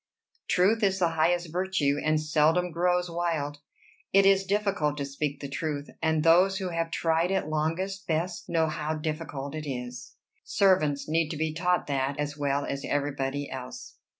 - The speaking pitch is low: No, medium, 160 Hz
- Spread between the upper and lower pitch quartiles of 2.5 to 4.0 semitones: Yes, average, 3.5 semitones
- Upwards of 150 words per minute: Yes, average, 170 wpm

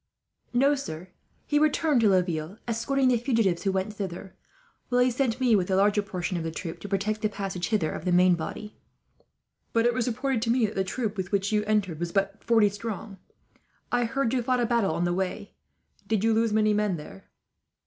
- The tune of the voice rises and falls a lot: No, average, 3.8 semitones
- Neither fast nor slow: No, fast, 215 wpm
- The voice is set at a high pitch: Yes, high, 210 Hz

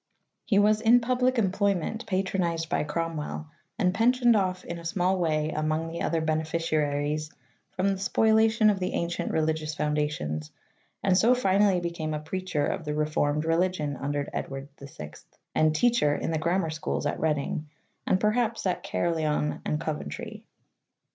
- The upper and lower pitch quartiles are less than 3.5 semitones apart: No, average, 4.5 semitones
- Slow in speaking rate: No, average, 155 wpm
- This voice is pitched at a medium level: Yes, medium, 165 Hz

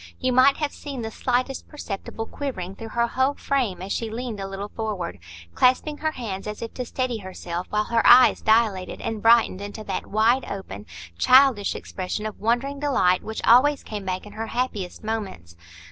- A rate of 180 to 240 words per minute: Yes, average, 185 wpm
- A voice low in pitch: No, high, 225 Hz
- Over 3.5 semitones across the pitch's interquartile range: Yes, average, 4.3 semitones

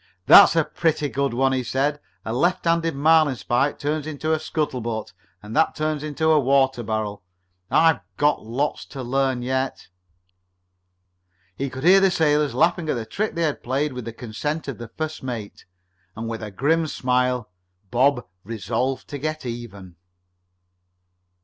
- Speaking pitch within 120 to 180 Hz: Yes, low, 135 Hz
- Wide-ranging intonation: No, average, 4.4 semitones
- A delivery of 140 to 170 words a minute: Yes, average, 155 wpm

